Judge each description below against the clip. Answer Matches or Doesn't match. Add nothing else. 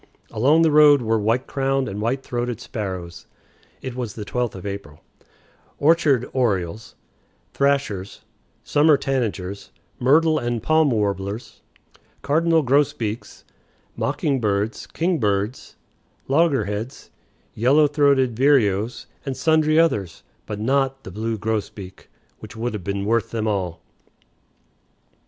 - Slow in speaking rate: Matches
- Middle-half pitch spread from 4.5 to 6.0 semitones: Matches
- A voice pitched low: Matches